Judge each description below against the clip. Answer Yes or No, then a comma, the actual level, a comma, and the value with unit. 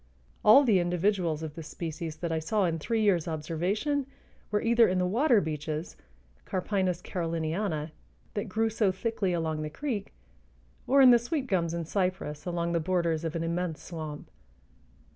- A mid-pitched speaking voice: Yes, medium, 180 Hz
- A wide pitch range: No, average, 4.5 semitones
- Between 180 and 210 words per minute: No, average, 165 wpm